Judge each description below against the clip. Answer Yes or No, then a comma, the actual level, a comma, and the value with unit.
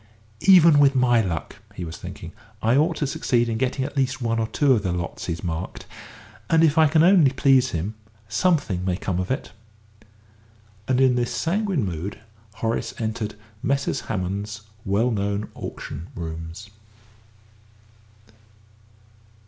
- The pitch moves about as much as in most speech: No, wide, 6.4 semitones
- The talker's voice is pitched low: Yes, low, 115 Hz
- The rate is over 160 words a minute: No, average, 150 wpm